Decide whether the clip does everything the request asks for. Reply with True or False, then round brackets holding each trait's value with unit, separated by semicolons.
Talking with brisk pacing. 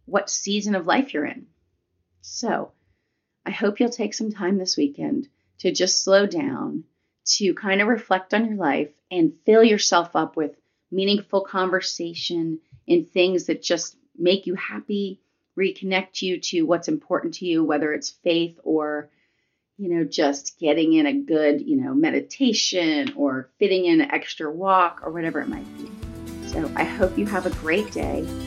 False (170 wpm)